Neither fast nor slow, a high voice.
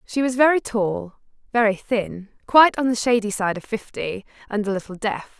Yes: average, 190 wpm; high, 220 Hz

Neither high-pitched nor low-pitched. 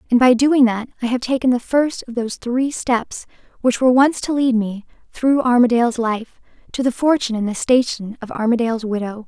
No: high, 245 Hz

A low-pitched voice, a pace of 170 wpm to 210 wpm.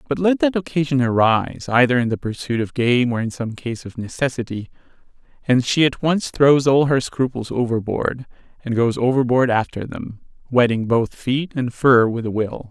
Yes: low, 125 Hz; average, 185 wpm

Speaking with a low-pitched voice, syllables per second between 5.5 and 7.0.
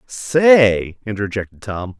No: low, 110 Hz; 3.4 syllables/s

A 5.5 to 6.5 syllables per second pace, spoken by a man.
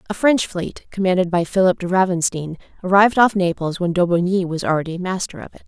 No: 6.0 syllables/s; female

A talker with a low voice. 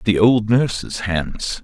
Yes: low, 105 Hz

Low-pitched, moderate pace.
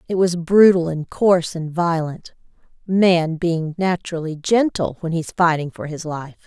No: medium, 170 Hz; average, 150 wpm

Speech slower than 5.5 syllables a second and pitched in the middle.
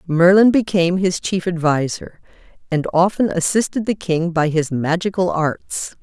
Yes: 4.5 syllables/s; medium, 175 Hz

